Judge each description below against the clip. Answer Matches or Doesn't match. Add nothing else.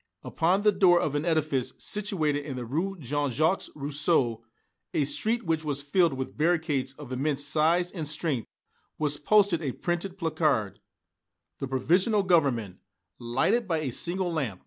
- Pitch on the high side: Doesn't match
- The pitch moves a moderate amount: Matches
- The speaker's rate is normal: Matches